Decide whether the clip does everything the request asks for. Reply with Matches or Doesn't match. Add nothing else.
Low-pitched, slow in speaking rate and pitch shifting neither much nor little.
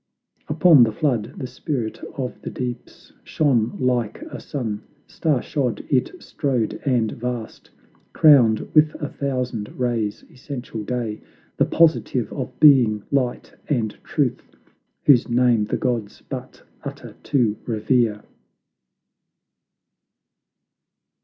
Matches